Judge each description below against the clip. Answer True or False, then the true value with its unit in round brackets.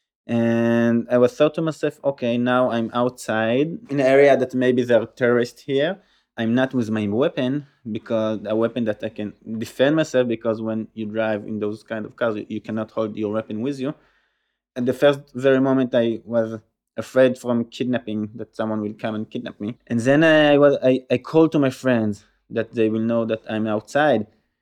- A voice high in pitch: False (115 Hz)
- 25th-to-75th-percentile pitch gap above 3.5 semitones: False (2.8 semitones)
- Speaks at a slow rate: False (200 wpm)